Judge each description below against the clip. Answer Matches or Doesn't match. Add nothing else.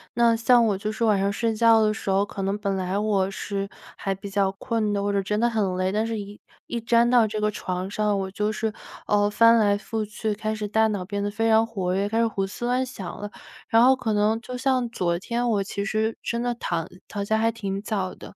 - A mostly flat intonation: Matches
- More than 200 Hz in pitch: Matches